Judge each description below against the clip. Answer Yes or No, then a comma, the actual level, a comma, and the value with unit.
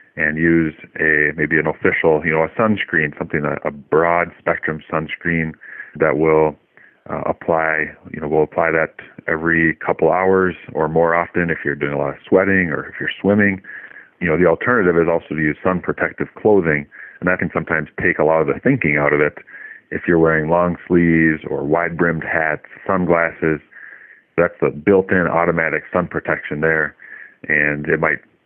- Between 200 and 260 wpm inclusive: No, average, 180 wpm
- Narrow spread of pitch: Yes, narrow, 2.0 semitones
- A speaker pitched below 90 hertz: Yes, very low, 80 Hz